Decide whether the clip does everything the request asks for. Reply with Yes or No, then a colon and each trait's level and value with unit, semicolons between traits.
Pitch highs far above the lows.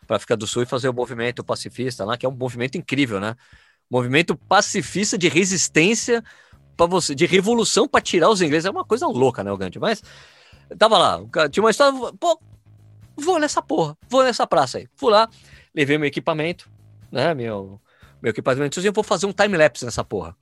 Yes: wide, 9.0 semitones